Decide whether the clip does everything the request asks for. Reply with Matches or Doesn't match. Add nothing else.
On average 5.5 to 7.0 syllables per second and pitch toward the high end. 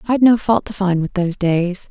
Doesn't match